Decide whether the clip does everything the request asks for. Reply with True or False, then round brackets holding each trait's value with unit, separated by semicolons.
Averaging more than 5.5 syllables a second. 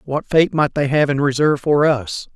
False (5.1 syllables/s)